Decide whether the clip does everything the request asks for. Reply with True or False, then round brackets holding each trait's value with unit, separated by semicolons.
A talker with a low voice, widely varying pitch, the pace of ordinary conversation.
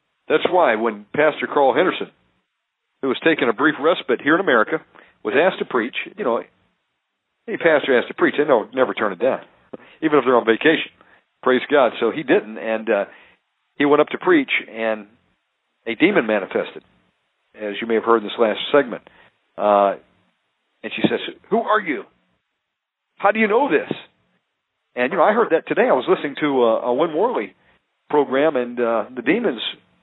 True (115 Hz; 6.5 semitones; 190 wpm)